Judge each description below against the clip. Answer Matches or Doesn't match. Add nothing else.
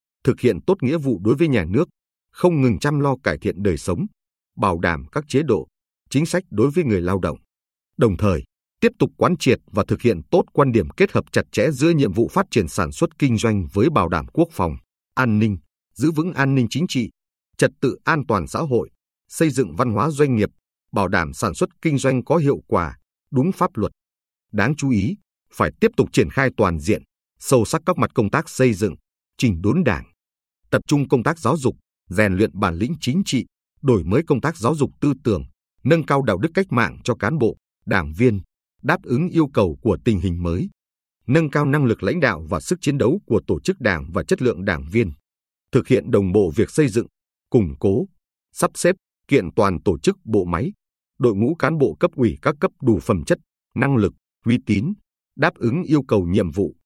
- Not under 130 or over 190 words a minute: Doesn't match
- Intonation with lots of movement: Matches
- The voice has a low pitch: Matches